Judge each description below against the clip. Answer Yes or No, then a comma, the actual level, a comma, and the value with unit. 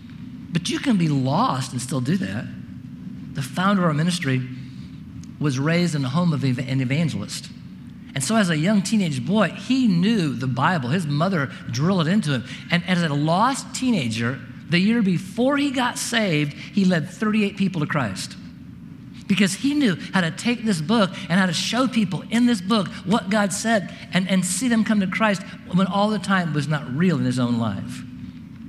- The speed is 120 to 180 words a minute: No, average, 195 wpm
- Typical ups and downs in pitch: No, wide, 6.3 semitones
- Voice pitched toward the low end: No, medium, 185 Hz